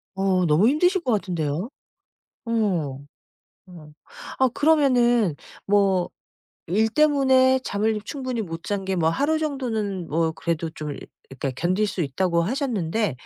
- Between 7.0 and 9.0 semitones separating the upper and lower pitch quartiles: Yes, wide, 7.4 semitones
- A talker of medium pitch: No, high, 200 Hz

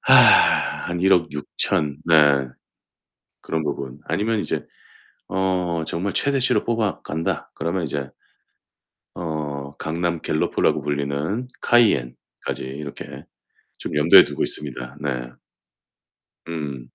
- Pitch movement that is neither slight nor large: Yes, average, 4.3 semitones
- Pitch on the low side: Yes, very low, 80 Hz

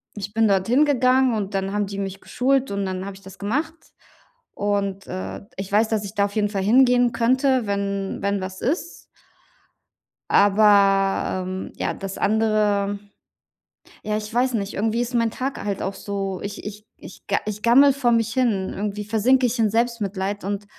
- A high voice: Yes, high, 210 Hz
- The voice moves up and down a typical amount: Yes, average, 3.2 semitones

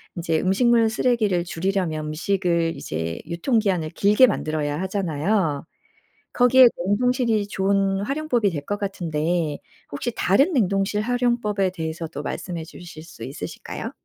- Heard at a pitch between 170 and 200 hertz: Yes, high, 190 Hz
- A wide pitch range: No, average, 5.0 semitones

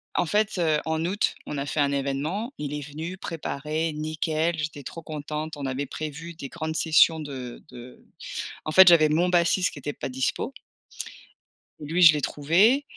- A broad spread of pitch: No, average, 2.8 semitones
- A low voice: No, medium, 155 Hz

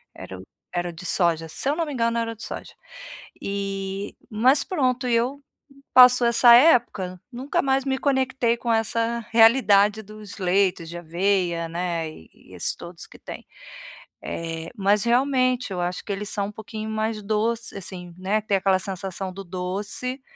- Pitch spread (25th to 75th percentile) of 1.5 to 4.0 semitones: No, average, 4.5 semitones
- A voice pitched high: Yes, high, 210 Hz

